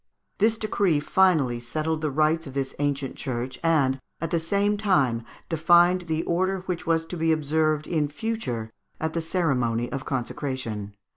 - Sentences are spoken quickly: No, average, 160 wpm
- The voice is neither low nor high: Yes, medium, 155 Hz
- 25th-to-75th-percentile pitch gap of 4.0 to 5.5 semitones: Yes, average, 4.6 semitones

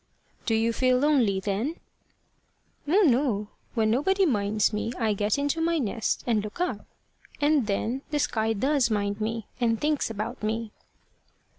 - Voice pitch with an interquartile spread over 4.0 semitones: Yes, average, 5.2 semitones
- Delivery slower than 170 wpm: Yes, average, 155 wpm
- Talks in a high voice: Yes, high, 230 Hz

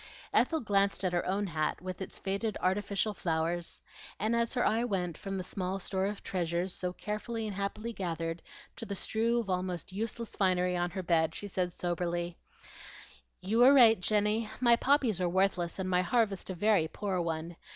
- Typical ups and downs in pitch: Yes, average, 3.3 semitones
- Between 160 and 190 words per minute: Yes, average, 185 wpm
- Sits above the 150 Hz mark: Yes, high, 190 Hz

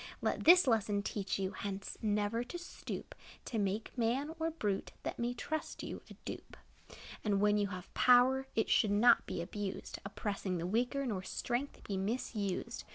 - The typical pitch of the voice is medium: No, high, 215 Hz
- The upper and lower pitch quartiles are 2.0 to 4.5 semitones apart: Yes, average, 3.7 semitones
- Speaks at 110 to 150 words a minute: No, average, 170 wpm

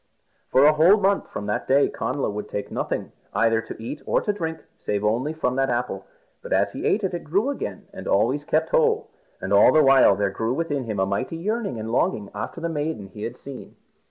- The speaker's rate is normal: No, fast, 220 wpm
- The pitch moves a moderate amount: No, wide, 7.0 semitones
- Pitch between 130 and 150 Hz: Yes, low, 135 Hz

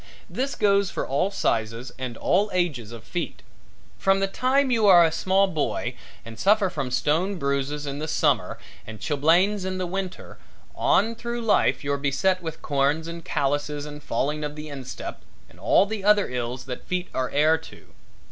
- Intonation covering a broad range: Yes, wide, 5.7 semitones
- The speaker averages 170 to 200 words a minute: Yes, average, 180 wpm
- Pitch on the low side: No, medium, 160 Hz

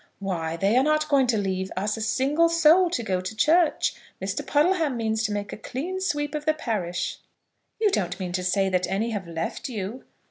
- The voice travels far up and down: Yes, wide, 8.0 semitones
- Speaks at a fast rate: Yes, fast, 210 wpm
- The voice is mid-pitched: No, high, 220 Hz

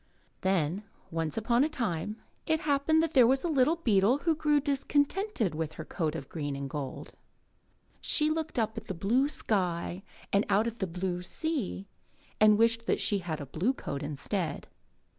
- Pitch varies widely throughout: Yes, wide, 8.6 semitones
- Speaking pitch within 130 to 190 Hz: No, high, 210 Hz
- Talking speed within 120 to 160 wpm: No, average, 180 wpm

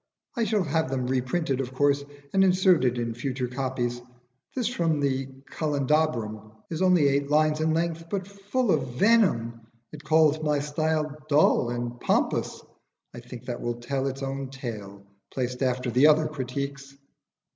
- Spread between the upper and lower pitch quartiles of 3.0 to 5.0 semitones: Yes, average, 4.0 semitones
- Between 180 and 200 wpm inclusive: No, average, 155 wpm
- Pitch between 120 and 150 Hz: Yes, medium, 140 Hz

